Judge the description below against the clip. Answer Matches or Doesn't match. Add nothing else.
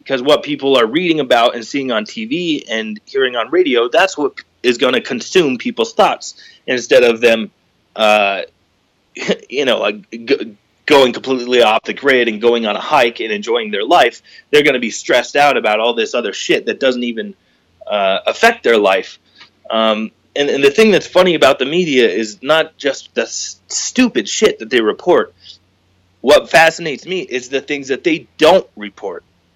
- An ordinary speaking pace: Matches